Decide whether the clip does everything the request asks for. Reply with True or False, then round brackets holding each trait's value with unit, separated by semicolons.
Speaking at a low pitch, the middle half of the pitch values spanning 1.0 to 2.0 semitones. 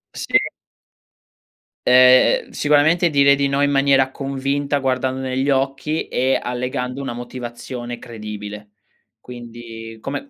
False (130 Hz; 2.4 semitones)